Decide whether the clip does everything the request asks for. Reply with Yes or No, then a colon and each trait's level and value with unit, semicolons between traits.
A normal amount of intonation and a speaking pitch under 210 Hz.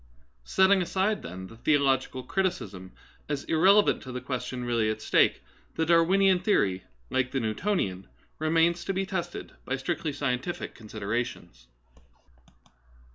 No: wide, 7.3 semitones; medium, 140 Hz